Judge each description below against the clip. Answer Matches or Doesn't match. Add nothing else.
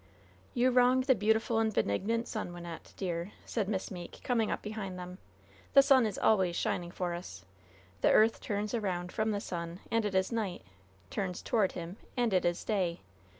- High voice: Matches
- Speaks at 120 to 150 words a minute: Doesn't match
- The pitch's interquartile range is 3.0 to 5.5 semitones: Matches